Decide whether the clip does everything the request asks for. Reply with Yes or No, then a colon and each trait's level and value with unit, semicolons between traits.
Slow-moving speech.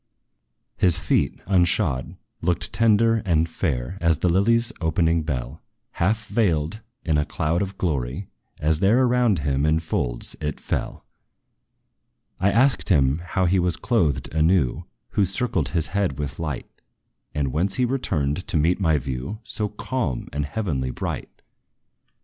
No: average, 145 wpm